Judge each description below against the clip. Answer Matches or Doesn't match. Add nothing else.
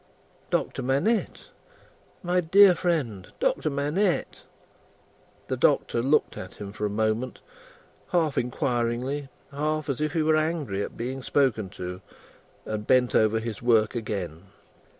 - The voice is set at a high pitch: Doesn't match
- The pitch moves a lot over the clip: Matches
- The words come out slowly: Matches